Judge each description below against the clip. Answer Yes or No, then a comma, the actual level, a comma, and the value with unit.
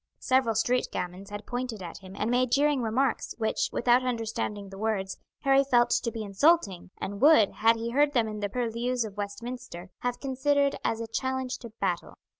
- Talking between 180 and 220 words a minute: Yes, average, 190 wpm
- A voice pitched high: Yes, high, 230 Hz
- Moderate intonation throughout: Yes, average, 3.7 semitones